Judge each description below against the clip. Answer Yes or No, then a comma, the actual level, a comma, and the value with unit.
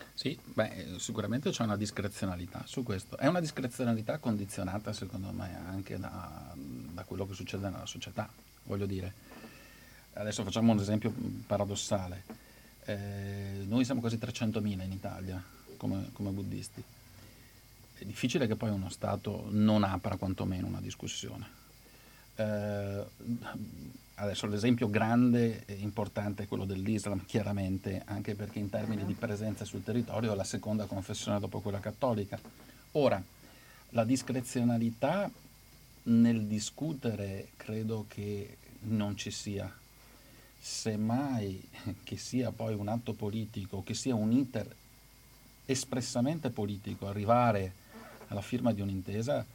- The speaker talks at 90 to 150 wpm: Yes, average, 125 wpm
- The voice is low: Yes, low, 110 Hz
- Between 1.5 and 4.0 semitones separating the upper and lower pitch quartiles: Yes, average, 2.9 semitones